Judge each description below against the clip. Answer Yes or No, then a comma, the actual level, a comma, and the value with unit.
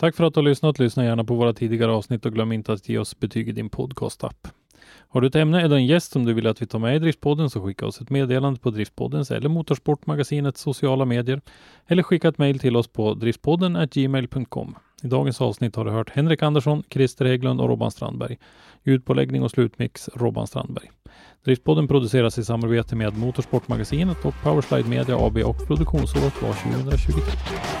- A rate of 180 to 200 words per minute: Yes, average, 190 wpm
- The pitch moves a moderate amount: Yes, average, 4.3 semitones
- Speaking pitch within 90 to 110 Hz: No, low, 130 Hz